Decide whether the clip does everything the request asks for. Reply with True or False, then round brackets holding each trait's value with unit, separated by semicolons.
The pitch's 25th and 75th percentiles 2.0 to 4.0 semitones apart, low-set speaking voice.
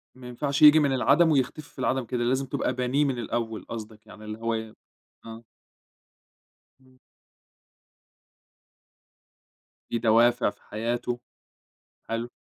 True (2.5 semitones; 120 Hz)